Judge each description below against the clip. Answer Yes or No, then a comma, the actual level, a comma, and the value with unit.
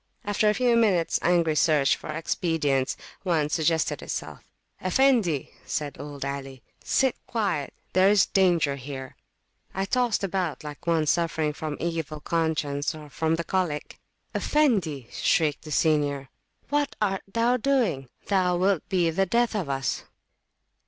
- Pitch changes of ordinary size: Yes, average, 4.8 semitones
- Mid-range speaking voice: Yes, medium, 165 Hz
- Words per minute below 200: Yes, average, 145 wpm